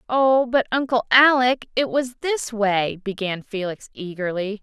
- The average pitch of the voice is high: Yes, high, 225 Hz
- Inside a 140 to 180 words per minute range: Yes, average, 145 wpm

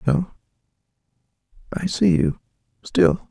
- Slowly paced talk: Yes, slow, 55 wpm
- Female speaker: No, male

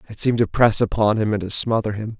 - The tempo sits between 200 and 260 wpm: No, fast, 275 wpm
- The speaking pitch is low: Yes, low, 110 Hz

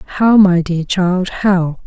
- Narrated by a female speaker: Yes, female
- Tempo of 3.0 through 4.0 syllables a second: Yes, 3.5 syllables/s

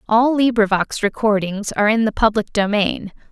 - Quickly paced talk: No, average, 145 wpm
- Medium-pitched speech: No, high, 215 Hz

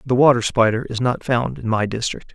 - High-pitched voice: No, low, 120 Hz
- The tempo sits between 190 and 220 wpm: No, fast, 230 wpm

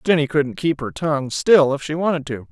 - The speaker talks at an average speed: No, fast, 240 wpm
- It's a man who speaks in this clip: Yes, male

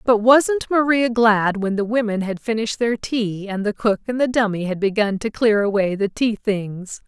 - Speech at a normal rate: No, fast, 210 wpm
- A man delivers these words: No, female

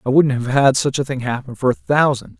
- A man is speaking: Yes, male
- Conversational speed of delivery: No, fast, 275 wpm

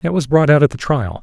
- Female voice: No, male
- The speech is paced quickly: Yes, fast, 340 wpm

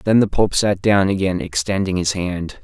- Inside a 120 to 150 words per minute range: No, fast, 205 wpm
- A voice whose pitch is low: Yes, very low, 95 Hz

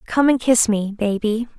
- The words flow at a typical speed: Yes, average, 190 wpm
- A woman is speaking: Yes, female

